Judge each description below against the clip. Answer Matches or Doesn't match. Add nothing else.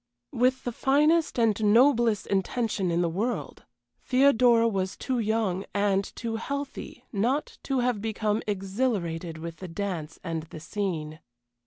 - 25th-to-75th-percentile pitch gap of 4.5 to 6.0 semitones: Matches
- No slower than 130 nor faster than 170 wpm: Matches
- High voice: Matches